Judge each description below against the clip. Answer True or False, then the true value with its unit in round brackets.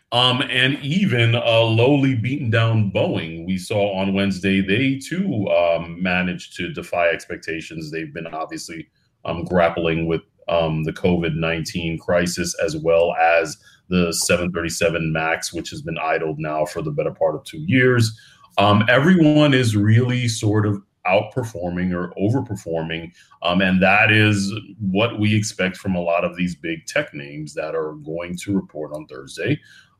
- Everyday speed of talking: True (160 wpm)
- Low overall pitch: True (95 Hz)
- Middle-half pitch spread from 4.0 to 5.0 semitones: True (4.7 semitones)